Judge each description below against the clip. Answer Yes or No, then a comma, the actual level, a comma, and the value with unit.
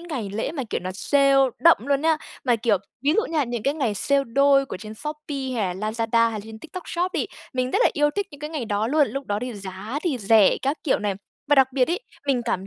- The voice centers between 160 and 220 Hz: No, very high, 265 Hz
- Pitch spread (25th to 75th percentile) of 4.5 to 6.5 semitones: Yes, average, 5.1 semitones